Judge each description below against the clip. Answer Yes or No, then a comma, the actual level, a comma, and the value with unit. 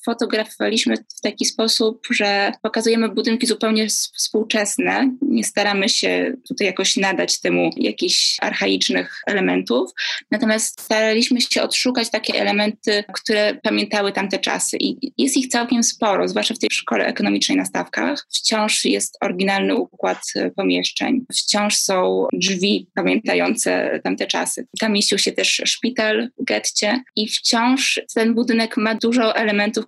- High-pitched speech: Yes, high, 220 Hz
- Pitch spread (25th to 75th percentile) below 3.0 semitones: Yes, narrow, 2.6 semitones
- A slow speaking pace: No, average, 135 wpm